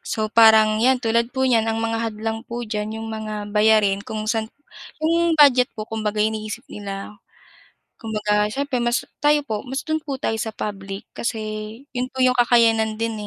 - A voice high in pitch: Yes, high, 225 Hz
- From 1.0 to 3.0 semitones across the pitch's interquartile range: Yes, narrow, 2.5 semitones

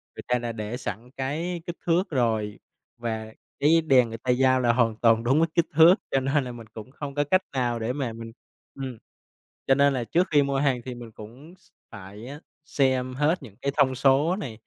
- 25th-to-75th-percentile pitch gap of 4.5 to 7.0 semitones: No, average, 3.6 semitones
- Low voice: Yes, low, 130 Hz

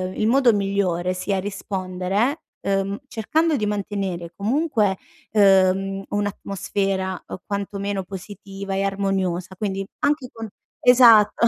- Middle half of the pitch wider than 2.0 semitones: No, narrow, 1.7 semitones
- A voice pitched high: Yes, high, 200 Hz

